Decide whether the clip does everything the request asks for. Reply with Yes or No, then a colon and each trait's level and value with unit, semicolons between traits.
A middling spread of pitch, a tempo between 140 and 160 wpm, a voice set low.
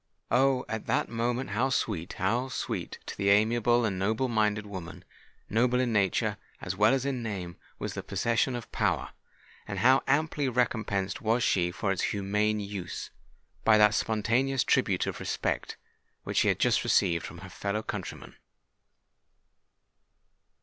Yes: average, 3.7 semitones; average, 145 wpm; low, 110 Hz